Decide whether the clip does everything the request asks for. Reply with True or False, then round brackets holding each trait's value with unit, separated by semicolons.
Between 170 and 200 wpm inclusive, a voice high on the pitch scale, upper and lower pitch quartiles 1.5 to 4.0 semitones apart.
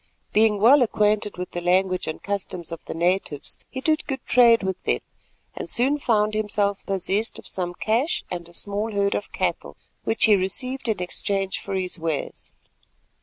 True (175 wpm; 200 Hz; 3.4 semitones)